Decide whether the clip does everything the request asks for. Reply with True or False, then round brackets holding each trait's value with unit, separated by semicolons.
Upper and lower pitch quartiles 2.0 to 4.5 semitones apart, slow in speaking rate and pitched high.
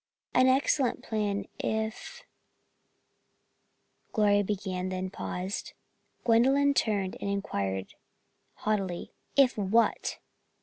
True (3.9 semitones; 90 wpm; 205 Hz)